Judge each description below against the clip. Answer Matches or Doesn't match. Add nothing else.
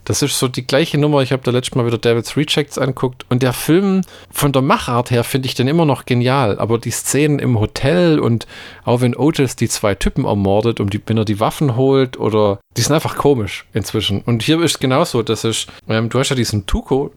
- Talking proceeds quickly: Matches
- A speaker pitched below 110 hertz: Doesn't match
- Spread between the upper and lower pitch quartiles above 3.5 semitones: Matches